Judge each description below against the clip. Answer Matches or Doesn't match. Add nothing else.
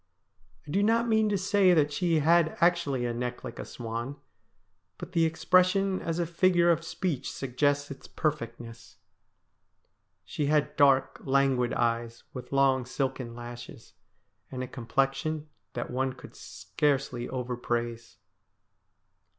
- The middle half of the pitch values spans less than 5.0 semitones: Doesn't match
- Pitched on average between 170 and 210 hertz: Doesn't match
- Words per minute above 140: Doesn't match